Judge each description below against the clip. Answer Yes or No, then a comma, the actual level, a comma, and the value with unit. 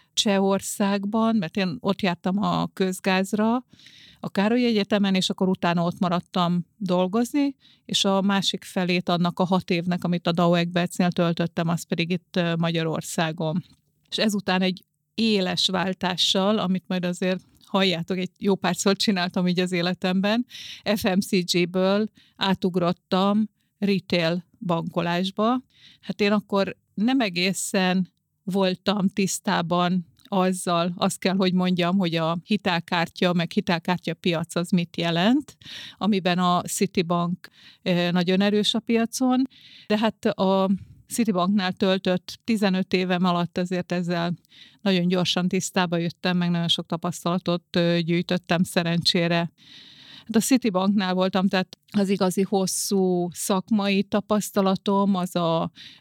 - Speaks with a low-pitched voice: No, medium, 185 Hz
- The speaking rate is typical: Yes, average, 120 wpm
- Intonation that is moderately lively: No, narrow, 2.3 semitones